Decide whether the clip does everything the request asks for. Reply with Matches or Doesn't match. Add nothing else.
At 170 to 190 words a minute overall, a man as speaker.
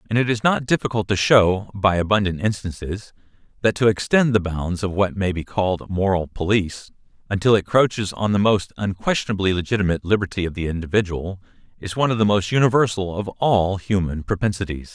Matches